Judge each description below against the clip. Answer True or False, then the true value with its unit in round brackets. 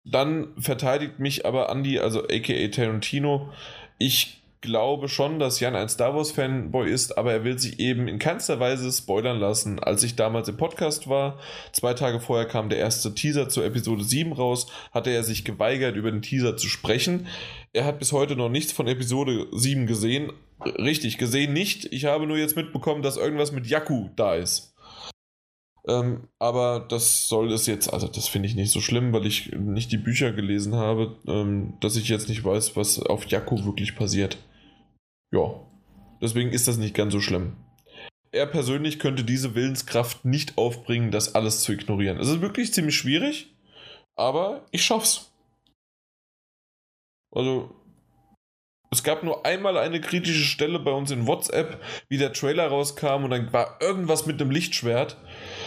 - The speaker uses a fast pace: False (170 wpm)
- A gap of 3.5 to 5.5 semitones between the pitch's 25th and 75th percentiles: True (4.4 semitones)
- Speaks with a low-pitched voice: True (125 Hz)